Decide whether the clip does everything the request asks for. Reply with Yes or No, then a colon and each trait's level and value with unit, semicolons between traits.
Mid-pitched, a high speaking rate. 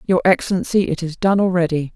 No: medium, 175 Hz; average, 185 wpm